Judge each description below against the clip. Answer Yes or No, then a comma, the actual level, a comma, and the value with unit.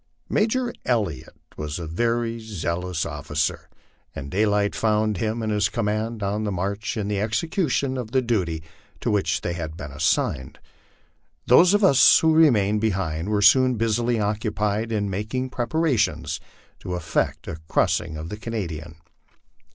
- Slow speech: No, average, 155 wpm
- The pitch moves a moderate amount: Yes, average, 4.7 semitones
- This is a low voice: Yes, low, 105 Hz